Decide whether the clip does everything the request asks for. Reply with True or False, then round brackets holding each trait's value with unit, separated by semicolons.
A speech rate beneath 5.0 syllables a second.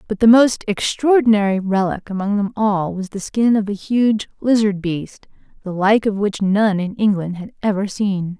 True (4.6 syllables/s)